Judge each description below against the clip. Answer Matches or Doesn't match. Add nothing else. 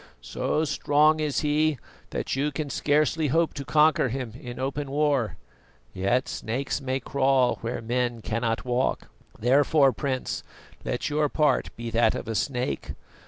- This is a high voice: Doesn't match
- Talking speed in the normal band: Matches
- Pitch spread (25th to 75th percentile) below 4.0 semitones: Matches